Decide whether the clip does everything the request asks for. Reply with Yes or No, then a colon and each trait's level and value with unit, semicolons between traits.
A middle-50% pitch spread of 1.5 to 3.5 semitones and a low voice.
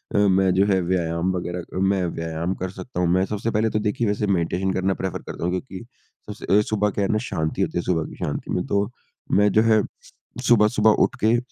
Yes: average, 2.8 semitones; very low, 95 Hz